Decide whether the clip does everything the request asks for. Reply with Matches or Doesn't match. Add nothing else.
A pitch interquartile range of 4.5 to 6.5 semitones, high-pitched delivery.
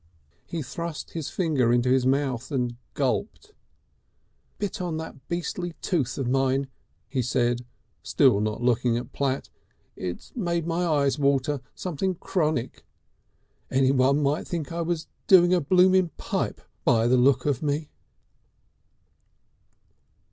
Doesn't match